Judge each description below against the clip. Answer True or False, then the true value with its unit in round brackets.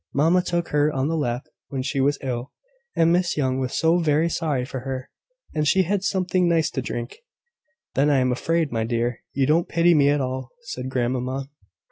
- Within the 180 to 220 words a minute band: True (200 wpm)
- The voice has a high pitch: False (140 Hz)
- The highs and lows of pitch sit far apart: False (4.2 semitones)